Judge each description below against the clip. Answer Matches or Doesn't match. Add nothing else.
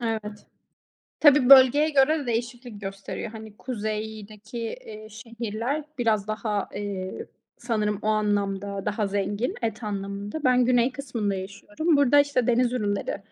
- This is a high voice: Matches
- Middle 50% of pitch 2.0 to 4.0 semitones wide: Matches